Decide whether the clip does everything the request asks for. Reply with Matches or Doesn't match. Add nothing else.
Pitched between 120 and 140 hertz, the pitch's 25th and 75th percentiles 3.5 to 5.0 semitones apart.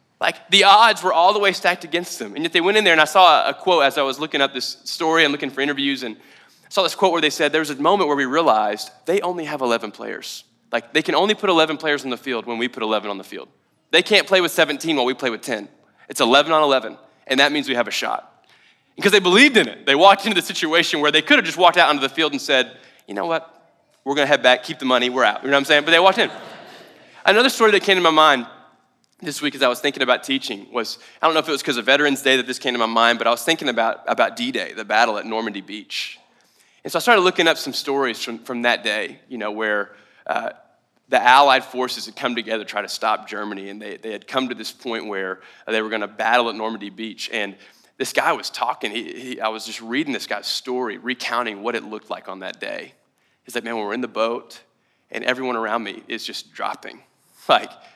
Doesn't match